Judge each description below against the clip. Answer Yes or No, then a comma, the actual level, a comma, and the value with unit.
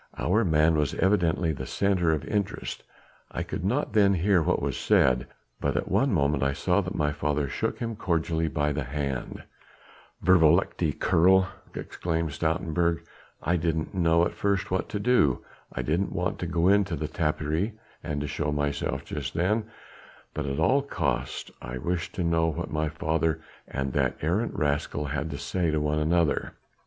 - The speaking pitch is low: Yes, very low, 80 Hz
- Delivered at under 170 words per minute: No, average, 175 wpm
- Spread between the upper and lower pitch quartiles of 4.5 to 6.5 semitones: No, average, 3.5 semitones